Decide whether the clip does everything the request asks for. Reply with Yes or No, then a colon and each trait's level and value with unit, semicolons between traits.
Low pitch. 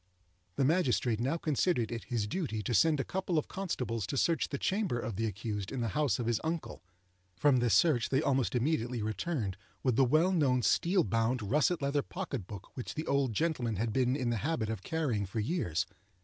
Yes: low, 125 Hz